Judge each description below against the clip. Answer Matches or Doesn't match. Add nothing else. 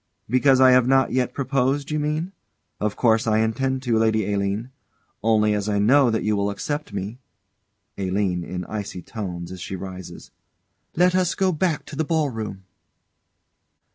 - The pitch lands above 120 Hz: Doesn't match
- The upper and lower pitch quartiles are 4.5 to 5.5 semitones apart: Matches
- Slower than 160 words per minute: Doesn't match